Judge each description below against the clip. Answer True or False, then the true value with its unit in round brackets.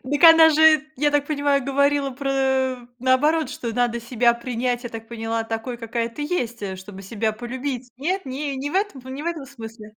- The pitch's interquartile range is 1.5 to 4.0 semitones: True (3.7 semitones)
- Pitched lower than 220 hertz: False (260 Hz)